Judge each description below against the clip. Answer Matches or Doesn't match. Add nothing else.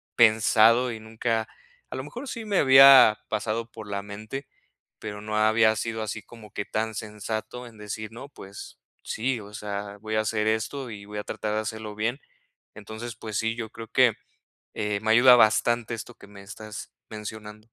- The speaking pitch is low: Matches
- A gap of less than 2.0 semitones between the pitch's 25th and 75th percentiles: Matches